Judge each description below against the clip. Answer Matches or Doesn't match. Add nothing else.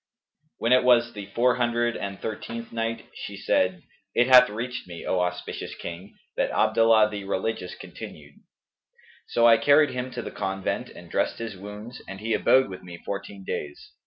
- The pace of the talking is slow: Doesn't match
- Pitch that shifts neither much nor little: Matches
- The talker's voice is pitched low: Matches